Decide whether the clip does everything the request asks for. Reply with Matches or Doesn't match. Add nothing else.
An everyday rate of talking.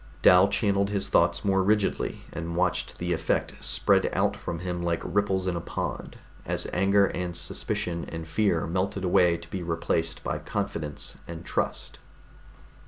Matches